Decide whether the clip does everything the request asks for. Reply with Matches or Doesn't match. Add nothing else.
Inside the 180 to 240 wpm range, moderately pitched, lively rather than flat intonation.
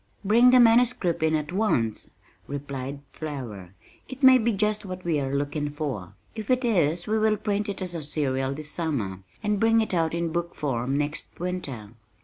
Matches